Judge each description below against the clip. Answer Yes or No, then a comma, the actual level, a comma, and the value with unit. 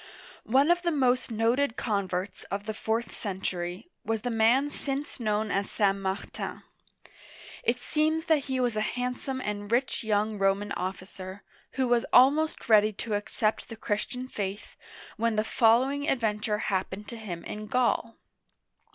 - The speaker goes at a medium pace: Yes, average, 155 wpm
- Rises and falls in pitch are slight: No, average, 3.7 semitones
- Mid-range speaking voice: No, high, 220 Hz